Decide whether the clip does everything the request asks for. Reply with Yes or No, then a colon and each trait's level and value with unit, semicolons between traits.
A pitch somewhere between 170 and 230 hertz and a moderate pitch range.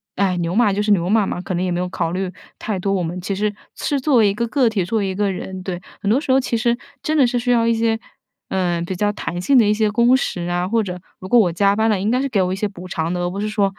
Yes: high, 200 Hz; average, 4.0 semitones